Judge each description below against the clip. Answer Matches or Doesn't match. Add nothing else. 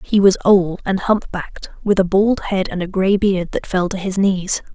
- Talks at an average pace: Doesn't match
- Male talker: Doesn't match